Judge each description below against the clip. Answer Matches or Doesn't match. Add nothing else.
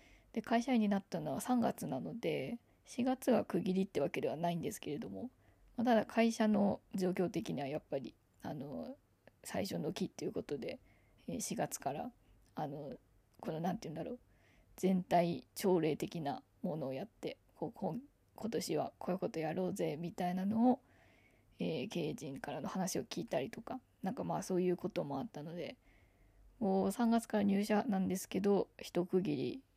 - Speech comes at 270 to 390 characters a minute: Matches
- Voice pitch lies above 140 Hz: Matches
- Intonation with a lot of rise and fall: Doesn't match